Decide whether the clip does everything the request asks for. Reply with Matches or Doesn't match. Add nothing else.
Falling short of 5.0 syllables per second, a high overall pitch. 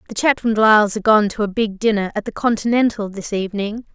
Doesn't match